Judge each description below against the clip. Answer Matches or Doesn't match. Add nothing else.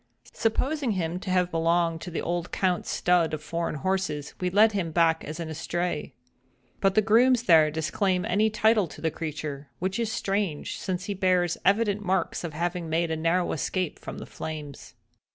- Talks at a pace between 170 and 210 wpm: Matches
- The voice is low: Doesn't match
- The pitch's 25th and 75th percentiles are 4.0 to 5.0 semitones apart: Doesn't match